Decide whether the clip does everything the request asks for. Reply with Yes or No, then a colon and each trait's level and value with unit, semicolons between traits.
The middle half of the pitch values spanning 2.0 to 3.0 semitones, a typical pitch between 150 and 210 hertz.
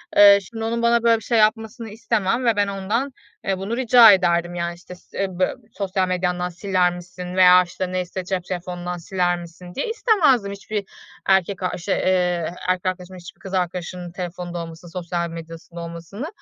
Yes: narrow, 2.6 semitones; medium, 185 Hz